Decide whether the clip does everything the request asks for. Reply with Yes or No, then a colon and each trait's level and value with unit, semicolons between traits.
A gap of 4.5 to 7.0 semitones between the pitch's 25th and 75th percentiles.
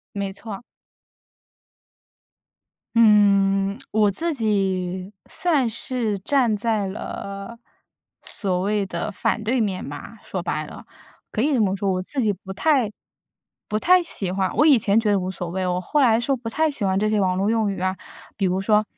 No: average, 3.2 semitones